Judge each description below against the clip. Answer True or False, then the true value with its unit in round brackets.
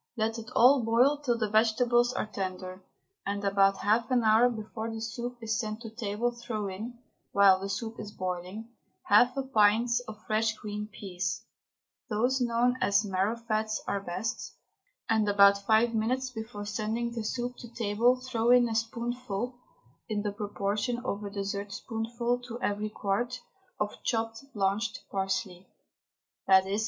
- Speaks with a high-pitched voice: True (220 Hz)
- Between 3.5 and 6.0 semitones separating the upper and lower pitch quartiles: False (2.7 semitones)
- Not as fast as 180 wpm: True (155 wpm)